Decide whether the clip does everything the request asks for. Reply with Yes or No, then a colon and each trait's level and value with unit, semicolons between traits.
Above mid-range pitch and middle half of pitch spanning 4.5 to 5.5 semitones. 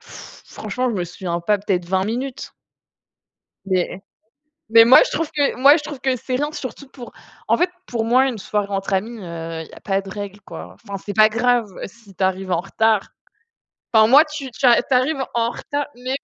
Yes: high, 225 Hz; average, 5.1 semitones